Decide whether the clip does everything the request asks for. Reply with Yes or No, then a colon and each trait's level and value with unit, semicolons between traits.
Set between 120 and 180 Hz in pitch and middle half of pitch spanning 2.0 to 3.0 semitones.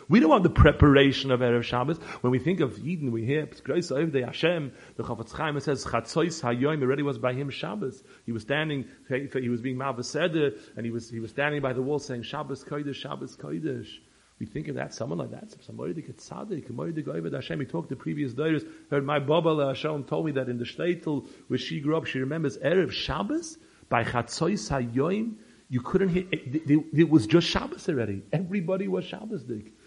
No: medium, 140 Hz; average, 4.0 semitones